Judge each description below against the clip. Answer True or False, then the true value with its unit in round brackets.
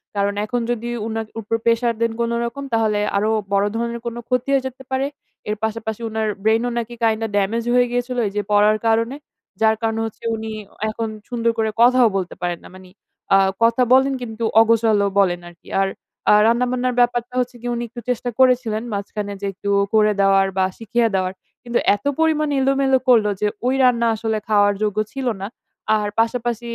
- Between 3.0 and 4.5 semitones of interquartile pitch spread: False (2.5 semitones)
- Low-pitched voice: False (230 Hz)